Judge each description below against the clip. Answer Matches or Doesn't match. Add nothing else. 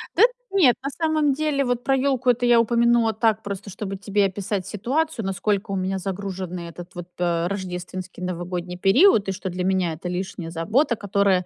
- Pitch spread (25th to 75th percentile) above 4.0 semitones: Matches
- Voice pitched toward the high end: Matches